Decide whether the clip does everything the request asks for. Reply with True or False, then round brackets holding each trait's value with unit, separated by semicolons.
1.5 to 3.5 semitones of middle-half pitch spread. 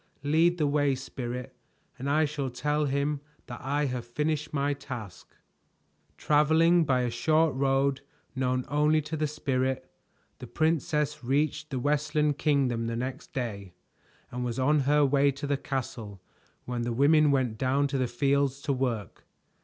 True (2.8 semitones)